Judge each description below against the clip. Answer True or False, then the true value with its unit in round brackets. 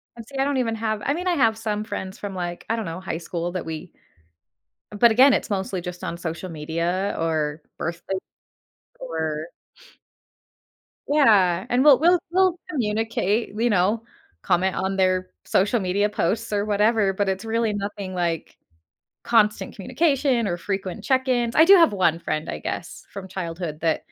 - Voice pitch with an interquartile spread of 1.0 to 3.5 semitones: False (4.6 semitones)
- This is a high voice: True (200 Hz)